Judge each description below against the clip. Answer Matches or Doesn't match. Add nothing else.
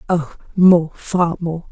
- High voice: Doesn't match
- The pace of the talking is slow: Matches